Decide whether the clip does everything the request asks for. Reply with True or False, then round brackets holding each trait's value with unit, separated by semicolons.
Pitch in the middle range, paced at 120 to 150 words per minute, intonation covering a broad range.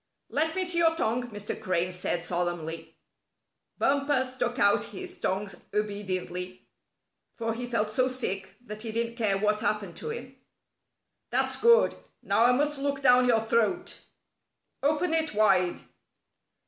False (230 Hz; 145 wpm; 6.1 semitones)